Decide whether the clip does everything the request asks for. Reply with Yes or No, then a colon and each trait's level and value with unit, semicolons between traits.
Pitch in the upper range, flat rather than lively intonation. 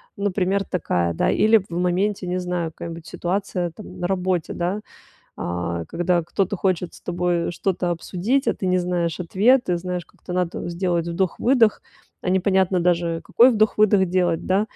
No: medium, 180 Hz; narrow, 2.1 semitones